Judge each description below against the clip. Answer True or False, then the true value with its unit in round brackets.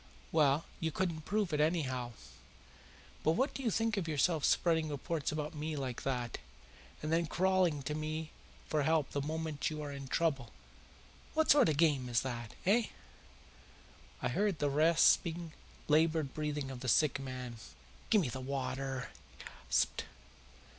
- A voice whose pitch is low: False (155 Hz)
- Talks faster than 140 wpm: True (160 wpm)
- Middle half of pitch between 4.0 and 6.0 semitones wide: False (3.4 semitones)